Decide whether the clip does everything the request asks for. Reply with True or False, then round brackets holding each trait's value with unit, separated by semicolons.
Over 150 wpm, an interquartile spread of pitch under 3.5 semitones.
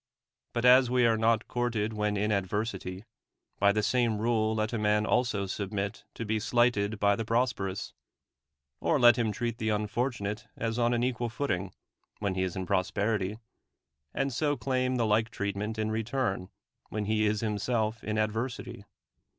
True (175 wpm; 2.5 semitones)